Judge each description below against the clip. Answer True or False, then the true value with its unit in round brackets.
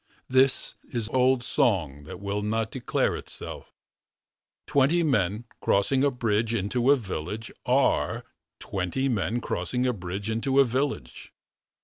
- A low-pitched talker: True (115 Hz)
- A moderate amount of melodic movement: True (4.6 semitones)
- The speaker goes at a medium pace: False (130 wpm)